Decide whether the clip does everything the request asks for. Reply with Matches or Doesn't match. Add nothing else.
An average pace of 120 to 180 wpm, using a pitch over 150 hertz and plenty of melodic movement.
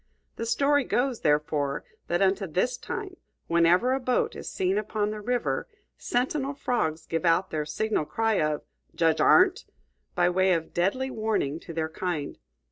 Matches